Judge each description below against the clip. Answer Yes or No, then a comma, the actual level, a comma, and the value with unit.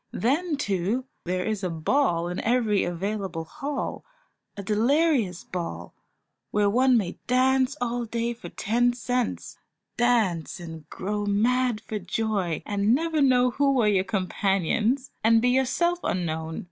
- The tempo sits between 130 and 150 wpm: Yes, average, 140 wpm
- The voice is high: Yes, high, 220 Hz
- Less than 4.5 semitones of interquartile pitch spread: No, average, 5.2 semitones